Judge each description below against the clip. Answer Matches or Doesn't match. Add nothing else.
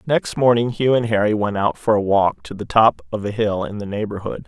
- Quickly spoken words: Matches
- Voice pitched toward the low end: Matches